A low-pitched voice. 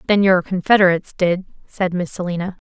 No: medium, 185 Hz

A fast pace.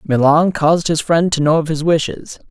Yes: fast, 215 wpm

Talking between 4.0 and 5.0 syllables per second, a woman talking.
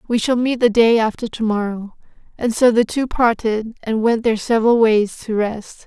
Yes: 4.8 syllables/s; female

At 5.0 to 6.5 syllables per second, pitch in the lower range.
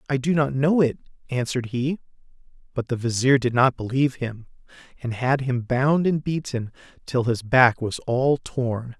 No: 4.7 syllables/s; low, 130 Hz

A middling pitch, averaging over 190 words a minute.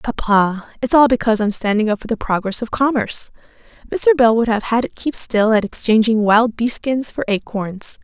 No: high, 225 Hz; average, 200 wpm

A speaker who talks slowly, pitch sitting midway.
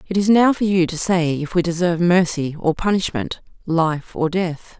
No: average, 200 wpm; medium, 175 Hz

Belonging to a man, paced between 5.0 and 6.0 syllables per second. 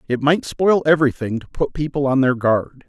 Yes: male; 5.2 syllables/s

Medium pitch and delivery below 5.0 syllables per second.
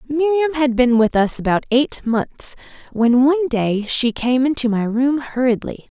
No: very high, 255 Hz; 4.3 syllables/s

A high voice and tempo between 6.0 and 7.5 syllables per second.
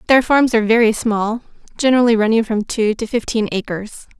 No: high, 225 Hz; 5.7 syllables/s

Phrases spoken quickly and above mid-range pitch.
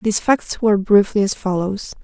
No: average, 175 wpm; high, 205 Hz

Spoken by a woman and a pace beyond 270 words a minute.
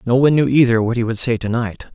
No: male; fast, 310 wpm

